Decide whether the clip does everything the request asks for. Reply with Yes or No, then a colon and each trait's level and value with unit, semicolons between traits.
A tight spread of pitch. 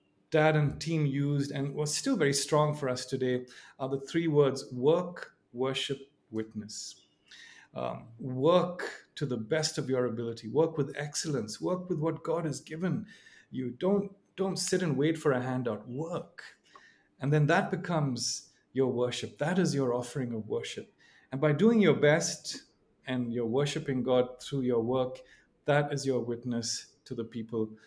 No: average, 4.1 semitones